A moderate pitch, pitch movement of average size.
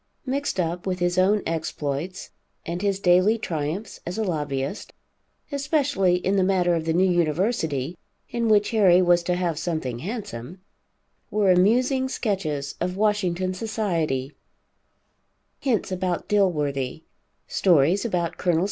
Yes: medium, 180 Hz; average, 4.0 semitones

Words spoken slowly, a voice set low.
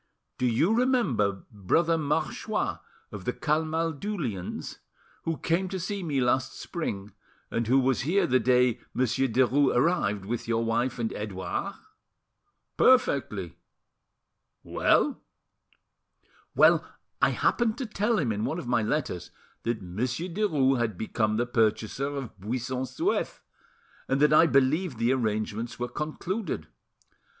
Yes: slow, 130 wpm; low, 130 Hz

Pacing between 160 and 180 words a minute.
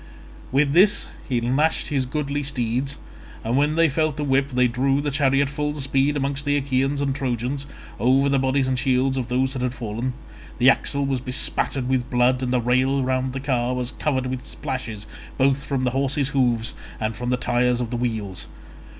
No: average, 195 wpm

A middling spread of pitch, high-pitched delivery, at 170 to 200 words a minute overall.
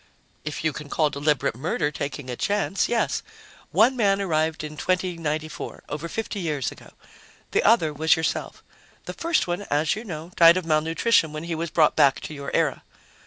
No: average, 3.5 semitones; medium, 160 Hz; average, 180 wpm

